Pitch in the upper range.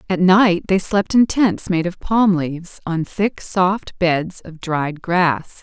No: medium, 180 Hz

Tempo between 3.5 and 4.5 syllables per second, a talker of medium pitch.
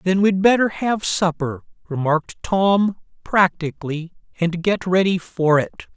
Yes: 4.4 syllables/s; medium, 180 Hz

